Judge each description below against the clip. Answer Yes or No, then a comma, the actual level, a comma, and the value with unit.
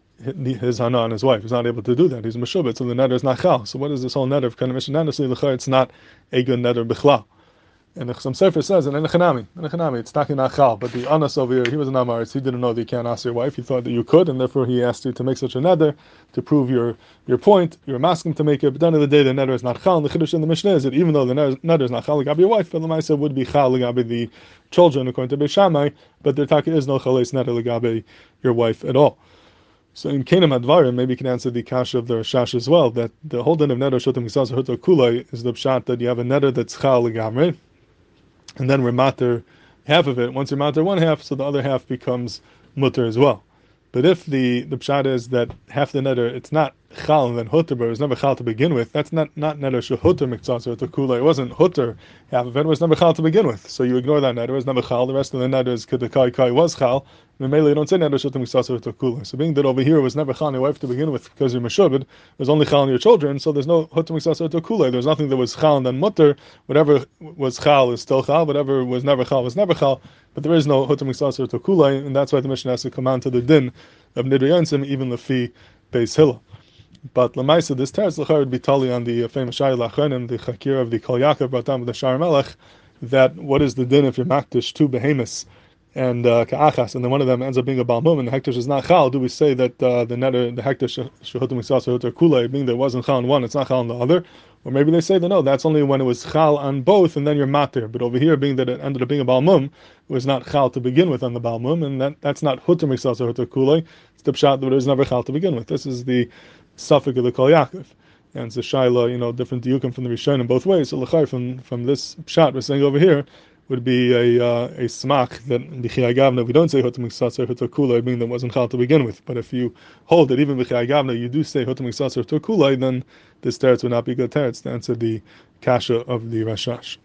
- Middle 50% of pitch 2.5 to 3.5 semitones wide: Yes, average, 3.1 semitones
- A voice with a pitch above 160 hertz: No, low, 130 Hz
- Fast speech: Yes, fast, 255 wpm